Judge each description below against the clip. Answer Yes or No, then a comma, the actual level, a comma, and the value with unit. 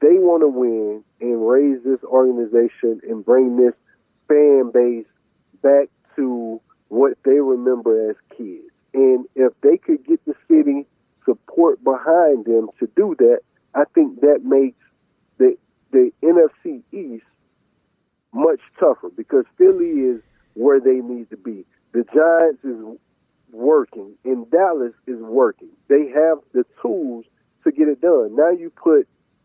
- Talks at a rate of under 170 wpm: Yes, average, 145 wpm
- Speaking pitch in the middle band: Yes, medium, 145 Hz